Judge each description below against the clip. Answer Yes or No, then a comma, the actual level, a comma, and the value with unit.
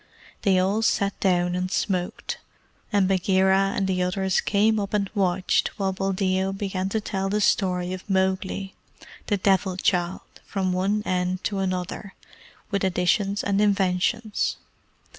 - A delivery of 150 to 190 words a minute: No, average, 140 wpm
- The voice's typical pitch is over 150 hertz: Yes, high, 190 Hz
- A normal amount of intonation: No, narrow, 1.4 semitones